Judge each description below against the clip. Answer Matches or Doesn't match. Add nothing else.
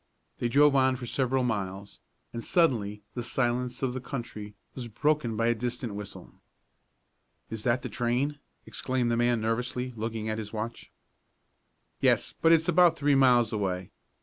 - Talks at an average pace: Matches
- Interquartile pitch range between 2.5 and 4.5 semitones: Matches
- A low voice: Matches